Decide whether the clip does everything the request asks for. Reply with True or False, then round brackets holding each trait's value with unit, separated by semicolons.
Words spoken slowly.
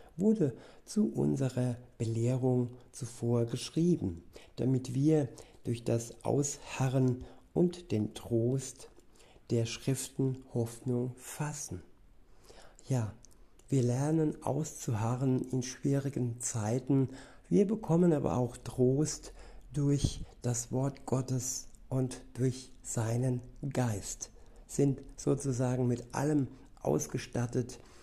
True (90 wpm)